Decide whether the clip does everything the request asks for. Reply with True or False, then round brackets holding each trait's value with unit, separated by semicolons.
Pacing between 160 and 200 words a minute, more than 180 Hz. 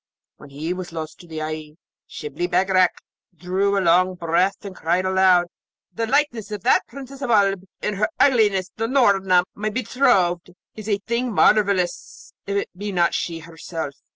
True (170 wpm; 190 Hz)